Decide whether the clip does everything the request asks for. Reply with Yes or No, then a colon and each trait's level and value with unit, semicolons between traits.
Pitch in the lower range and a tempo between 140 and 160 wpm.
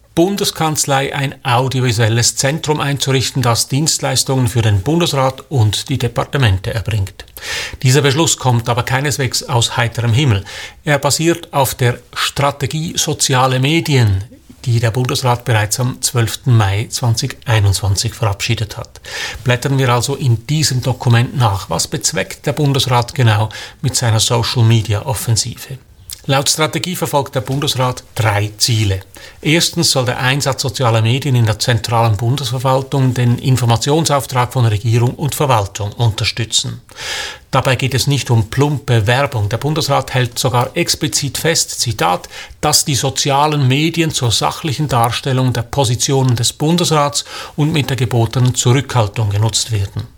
No: low, 125 Hz; average, 130 wpm